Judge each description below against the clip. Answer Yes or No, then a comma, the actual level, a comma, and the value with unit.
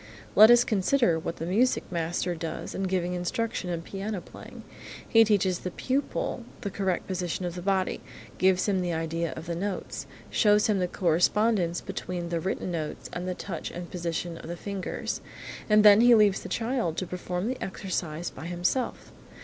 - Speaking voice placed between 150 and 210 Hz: Yes, medium, 185 Hz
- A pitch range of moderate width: Yes, average, 3.2 semitones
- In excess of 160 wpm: Yes, average, 185 wpm